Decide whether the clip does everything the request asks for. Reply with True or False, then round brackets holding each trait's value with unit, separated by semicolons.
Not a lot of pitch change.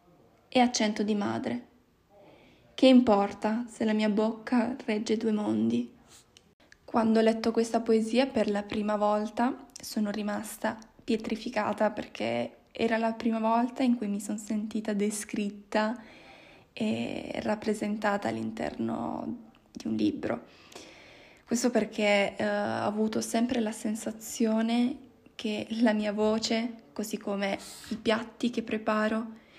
True (1.7 semitones)